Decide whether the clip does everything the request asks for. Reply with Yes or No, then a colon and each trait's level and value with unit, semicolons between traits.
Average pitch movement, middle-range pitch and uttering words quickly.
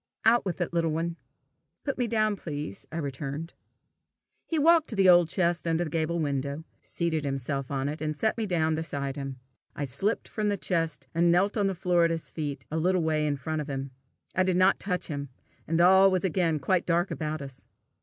Yes: average, 4.0 semitones; medium, 165 Hz; fast, 215 wpm